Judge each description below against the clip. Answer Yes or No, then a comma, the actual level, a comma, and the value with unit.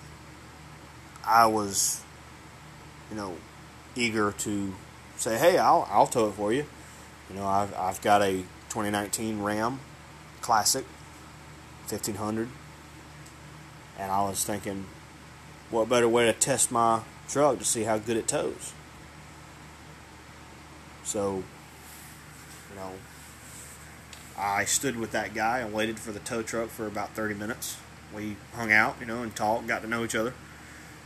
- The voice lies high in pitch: No, low, 105 Hz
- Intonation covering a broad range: Yes, wide, 6.3 semitones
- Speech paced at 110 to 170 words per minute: Yes, slow, 135 wpm